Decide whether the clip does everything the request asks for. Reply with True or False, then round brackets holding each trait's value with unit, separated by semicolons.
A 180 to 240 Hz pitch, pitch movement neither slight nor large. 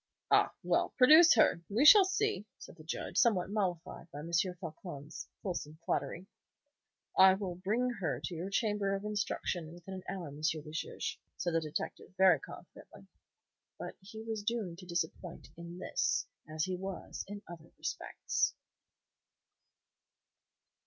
True (185 Hz; 3.7 semitones)